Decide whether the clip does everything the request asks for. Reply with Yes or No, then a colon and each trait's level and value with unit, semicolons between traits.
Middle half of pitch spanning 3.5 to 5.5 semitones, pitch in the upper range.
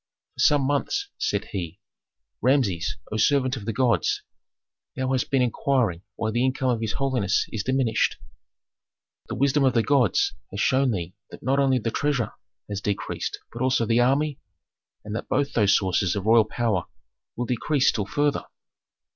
No: average, 4.1 semitones; low, 125 Hz